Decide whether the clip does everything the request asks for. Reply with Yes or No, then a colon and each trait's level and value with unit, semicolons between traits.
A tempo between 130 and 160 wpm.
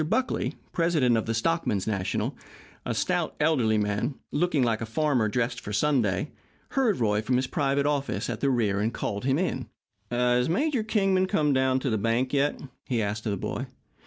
No: average, 185 wpm